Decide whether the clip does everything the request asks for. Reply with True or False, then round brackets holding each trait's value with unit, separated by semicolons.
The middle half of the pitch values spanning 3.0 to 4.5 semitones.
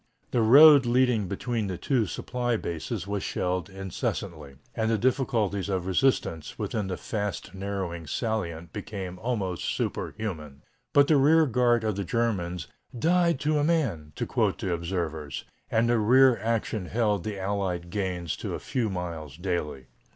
False (5.2 semitones)